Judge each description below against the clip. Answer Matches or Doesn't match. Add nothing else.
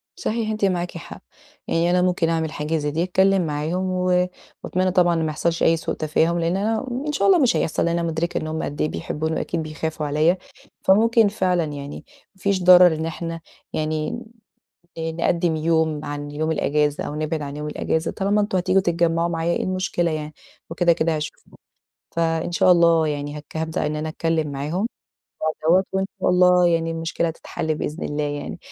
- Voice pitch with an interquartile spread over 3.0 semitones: Doesn't match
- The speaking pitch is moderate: Matches